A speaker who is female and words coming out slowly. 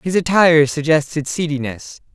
No: male; slow, 110 wpm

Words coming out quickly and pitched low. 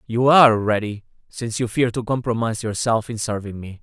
No: average, 190 wpm; low, 115 Hz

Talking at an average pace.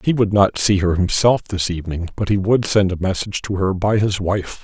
No: fast, 245 wpm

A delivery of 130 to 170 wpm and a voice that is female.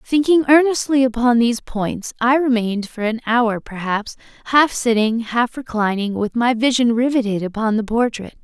Yes: average, 155 wpm; female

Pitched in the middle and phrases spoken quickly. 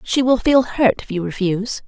No: high, 225 Hz; fast, 225 wpm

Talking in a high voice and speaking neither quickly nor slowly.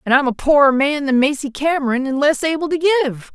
No: very high, 285 Hz; fast, 235 wpm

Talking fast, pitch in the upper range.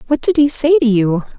Yes: fast, 260 wpm; very high, 250 Hz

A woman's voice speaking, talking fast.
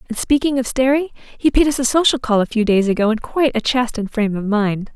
Yes: female; fast, 255 wpm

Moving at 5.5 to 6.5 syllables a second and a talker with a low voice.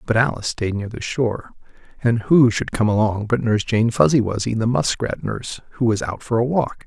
Yes: 5.6 syllables/s; low, 115 Hz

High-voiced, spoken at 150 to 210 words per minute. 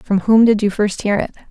No: high, 205 Hz; fast, 280 wpm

